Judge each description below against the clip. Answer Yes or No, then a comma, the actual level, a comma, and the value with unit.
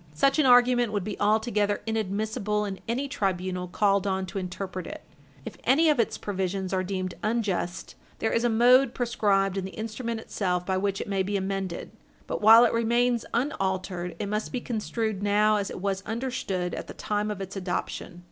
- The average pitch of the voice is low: No, high, 205 Hz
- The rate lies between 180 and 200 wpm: Yes, average, 190 wpm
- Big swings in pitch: No, average, 3.3 semitones